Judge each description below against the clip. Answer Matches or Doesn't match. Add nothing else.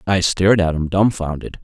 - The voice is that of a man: Matches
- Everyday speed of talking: Matches